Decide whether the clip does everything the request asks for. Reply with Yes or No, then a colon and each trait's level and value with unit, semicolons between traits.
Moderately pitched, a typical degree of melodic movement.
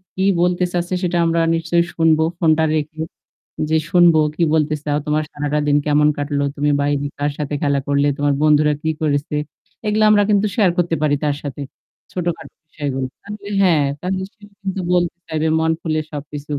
Yes: medium, 155 Hz; average, 3.1 semitones